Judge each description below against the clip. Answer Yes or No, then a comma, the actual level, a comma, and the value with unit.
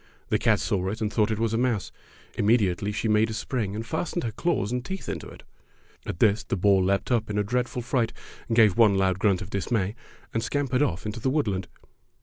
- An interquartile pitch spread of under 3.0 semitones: No, average, 3.3 semitones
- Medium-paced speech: No, fast, 225 wpm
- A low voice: Yes, low, 110 Hz